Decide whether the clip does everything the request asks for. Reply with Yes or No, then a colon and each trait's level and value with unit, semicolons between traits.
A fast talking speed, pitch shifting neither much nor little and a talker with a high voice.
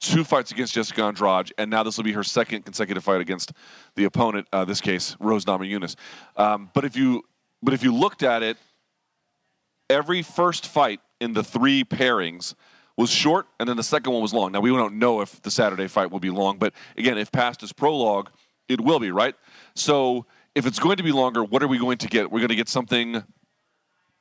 No: fast, 220 wpm; average, 4.4 semitones; low, 115 Hz